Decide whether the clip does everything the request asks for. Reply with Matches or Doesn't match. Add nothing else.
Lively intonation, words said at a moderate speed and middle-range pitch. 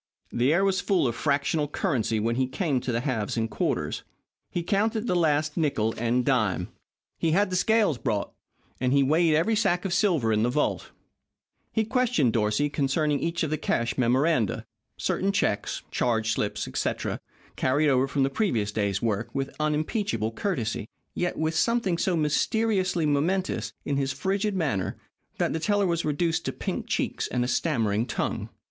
Matches